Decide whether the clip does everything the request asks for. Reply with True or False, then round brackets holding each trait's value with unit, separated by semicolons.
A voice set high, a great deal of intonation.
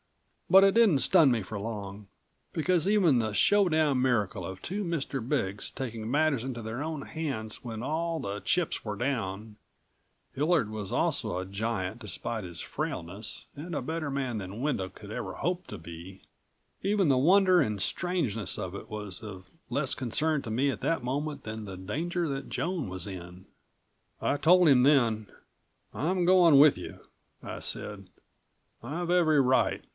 False (130 Hz; 7.3 semitones)